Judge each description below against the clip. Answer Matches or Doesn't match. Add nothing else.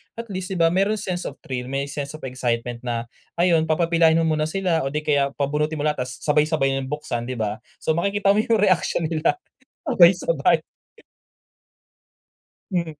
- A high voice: Doesn't match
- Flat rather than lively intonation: Doesn't match